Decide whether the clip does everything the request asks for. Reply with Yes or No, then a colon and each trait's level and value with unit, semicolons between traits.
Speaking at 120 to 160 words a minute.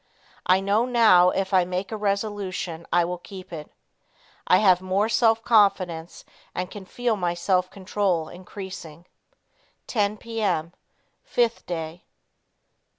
Yes: slow, 135 wpm